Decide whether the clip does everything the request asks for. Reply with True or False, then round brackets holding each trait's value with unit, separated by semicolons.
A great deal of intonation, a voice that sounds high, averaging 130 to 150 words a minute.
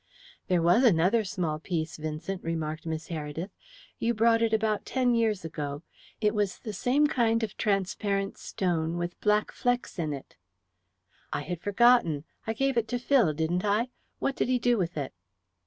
False (5.8 semitones; 195 Hz; 170 wpm)